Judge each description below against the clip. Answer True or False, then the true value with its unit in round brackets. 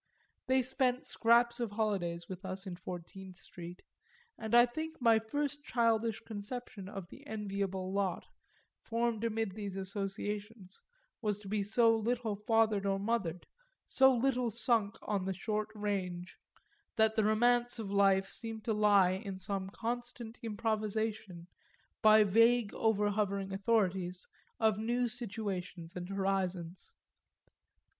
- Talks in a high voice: True (210 Hz)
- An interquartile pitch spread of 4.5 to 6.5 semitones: False (3.0 semitones)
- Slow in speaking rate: True (130 wpm)